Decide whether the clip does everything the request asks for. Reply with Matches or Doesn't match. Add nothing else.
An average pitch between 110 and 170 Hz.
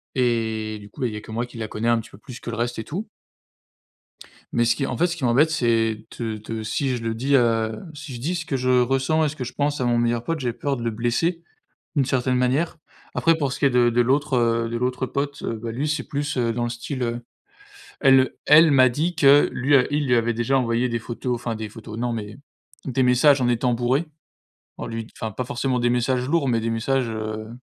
Matches